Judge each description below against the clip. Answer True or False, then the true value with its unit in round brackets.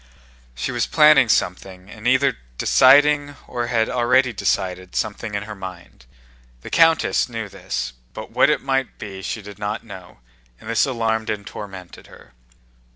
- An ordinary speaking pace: True (160 wpm)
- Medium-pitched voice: False (110 Hz)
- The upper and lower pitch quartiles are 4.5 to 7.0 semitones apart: True (5.1 semitones)